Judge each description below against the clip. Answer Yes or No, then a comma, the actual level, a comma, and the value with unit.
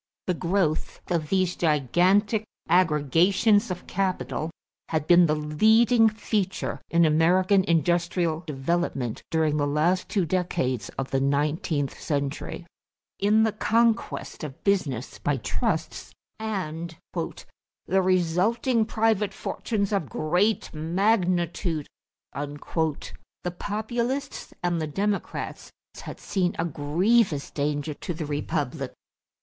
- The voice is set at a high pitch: No, medium, 175 Hz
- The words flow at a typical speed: No, slow, 110 wpm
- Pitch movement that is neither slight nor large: Yes, average, 4.9 semitones